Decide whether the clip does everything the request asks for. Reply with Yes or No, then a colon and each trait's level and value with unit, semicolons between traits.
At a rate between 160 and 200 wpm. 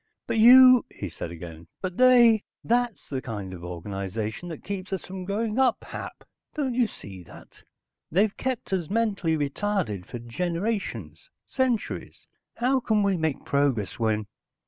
No: average, 150 wpm